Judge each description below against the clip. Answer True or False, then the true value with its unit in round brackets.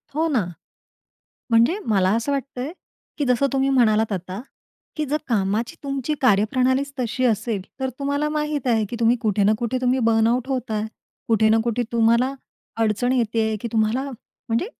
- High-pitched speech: True (235 Hz)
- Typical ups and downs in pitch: True (3.3 semitones)